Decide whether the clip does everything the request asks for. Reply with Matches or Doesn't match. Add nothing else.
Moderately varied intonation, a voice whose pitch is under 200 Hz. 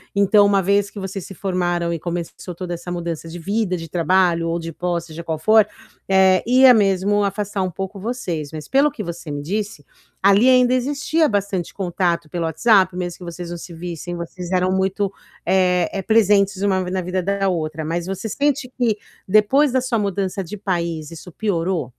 Matches